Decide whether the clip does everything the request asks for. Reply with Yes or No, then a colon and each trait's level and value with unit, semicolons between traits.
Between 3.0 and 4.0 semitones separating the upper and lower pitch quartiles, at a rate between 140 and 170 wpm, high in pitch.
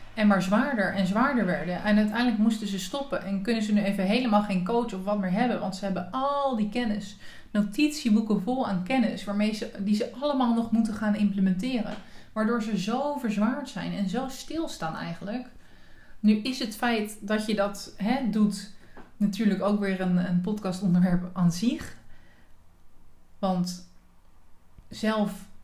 Yes: average, 3.4 semitones; average, 165 wpm; high, 210 Hz